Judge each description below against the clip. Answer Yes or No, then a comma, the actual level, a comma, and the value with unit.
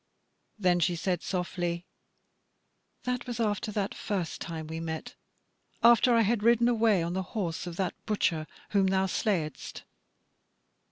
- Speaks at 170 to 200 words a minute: No, average, 145 wpm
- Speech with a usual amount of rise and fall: Yes, average, 4.2 semitones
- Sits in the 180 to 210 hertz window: Yes, high, 190 Hz